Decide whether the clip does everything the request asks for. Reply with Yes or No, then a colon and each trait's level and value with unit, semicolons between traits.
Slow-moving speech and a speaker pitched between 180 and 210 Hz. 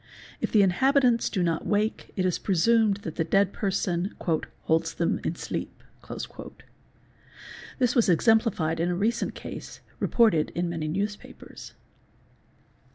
Yes: slow, 130 wpm; high, 190 Hz